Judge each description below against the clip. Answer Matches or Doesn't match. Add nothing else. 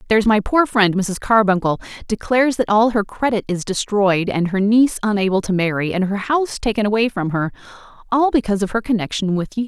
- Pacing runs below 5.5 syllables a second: Doesn't match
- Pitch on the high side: Matches